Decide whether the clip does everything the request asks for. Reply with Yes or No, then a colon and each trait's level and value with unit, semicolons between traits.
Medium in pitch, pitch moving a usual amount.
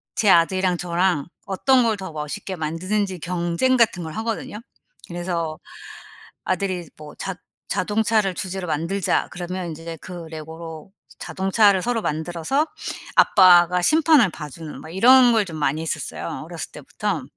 Yes: medium, 180 Hz; average, 3.7 semitones